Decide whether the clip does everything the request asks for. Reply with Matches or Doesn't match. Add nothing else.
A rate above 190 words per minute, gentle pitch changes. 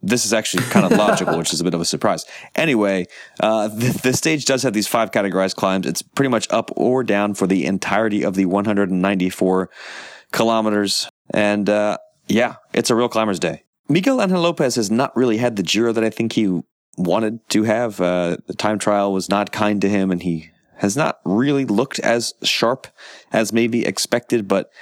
Doesn't match